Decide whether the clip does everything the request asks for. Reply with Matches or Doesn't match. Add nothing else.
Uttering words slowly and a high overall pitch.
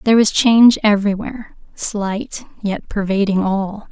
Matches